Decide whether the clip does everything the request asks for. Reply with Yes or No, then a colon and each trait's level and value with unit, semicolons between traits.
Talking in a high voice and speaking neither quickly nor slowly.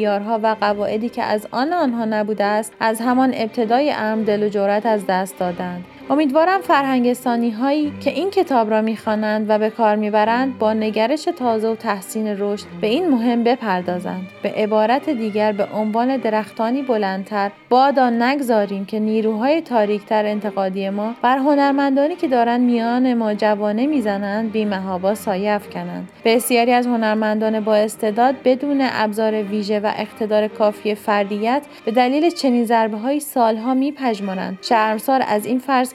Yes: high, 220 Hz; average, 145 wpm